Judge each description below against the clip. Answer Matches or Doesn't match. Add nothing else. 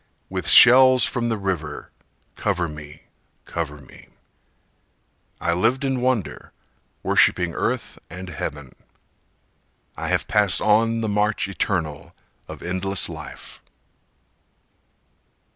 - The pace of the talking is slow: Matches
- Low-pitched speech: Matches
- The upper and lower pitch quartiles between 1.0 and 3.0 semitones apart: Doesn't match